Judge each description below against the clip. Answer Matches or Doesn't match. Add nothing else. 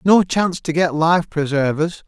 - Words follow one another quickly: Doesn't match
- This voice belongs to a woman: Doesn't match